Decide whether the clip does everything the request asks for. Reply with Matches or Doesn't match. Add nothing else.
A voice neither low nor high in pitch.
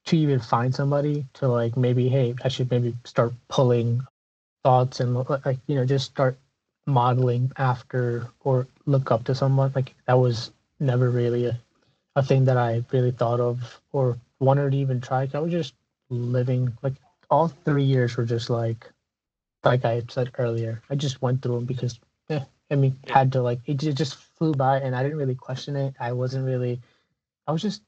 Doesn't match